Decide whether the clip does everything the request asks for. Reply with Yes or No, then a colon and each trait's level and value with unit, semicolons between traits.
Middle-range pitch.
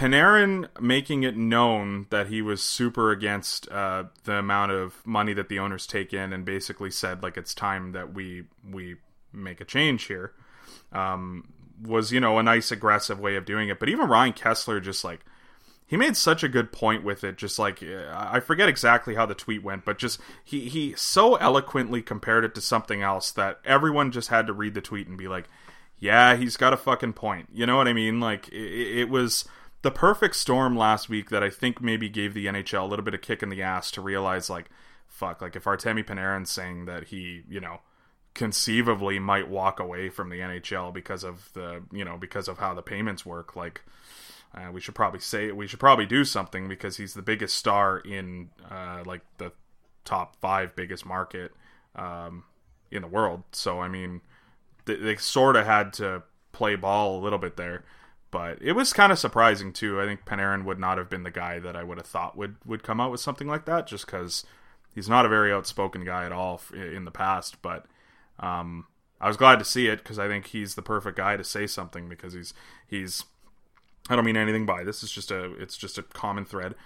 No: low, 100 Hz